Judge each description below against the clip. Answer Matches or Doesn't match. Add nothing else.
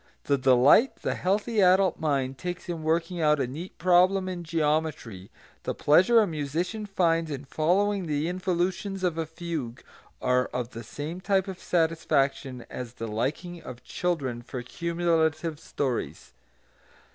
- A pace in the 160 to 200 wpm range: Doesn't match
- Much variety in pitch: Doesn't match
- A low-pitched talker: Doesn't match